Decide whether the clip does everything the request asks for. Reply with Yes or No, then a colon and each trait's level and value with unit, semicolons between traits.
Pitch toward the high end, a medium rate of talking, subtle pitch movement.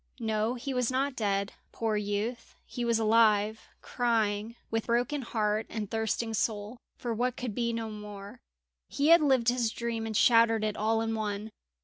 Yes: high, 225 Hz; average, 170 wpm; narrow, 2.0 semitones